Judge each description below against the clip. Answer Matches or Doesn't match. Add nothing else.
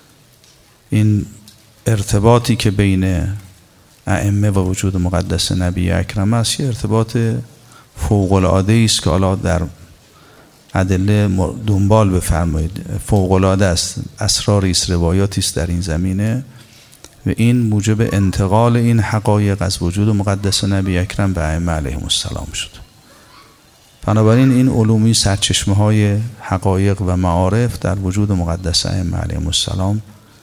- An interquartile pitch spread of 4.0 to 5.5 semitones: Doesn't match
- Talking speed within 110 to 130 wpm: Matches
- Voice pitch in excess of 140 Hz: Doesn't match